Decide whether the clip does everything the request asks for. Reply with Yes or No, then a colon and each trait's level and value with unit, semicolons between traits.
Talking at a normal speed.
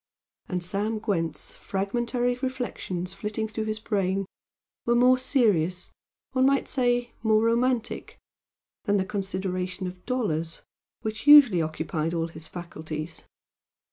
No: slow, 120 wpm